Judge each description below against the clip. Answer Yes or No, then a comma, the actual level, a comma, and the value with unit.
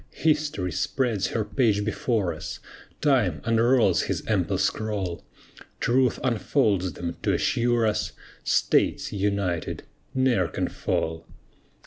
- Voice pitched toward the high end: No, low, 110 Hz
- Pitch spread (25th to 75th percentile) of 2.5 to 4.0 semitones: No, average, 4.9 semitones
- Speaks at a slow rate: Yes, slow, 110 wpm